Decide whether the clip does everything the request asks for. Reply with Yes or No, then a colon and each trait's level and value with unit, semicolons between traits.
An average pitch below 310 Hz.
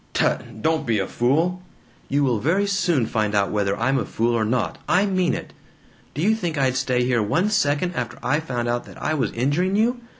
Yes: low, 135 Hz